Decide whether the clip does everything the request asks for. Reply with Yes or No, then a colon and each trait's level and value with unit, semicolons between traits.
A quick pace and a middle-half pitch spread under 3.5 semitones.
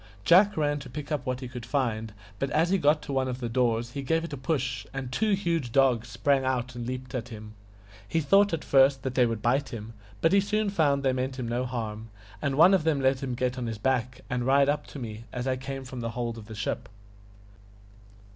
Yes: fast, 250 wpm; average, 3.1 semitones